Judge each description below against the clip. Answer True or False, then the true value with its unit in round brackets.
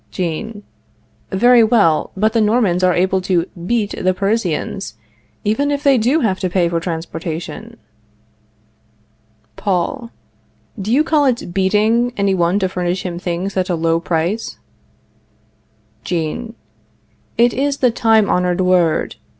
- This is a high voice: True (195 Hz)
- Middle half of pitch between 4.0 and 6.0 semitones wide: True (4.6 semitones)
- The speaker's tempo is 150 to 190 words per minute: False (135 wpm)